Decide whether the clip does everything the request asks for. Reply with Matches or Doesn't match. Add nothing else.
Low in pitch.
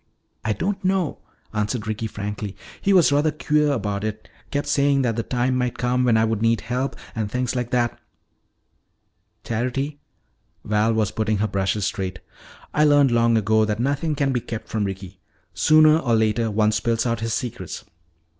Matches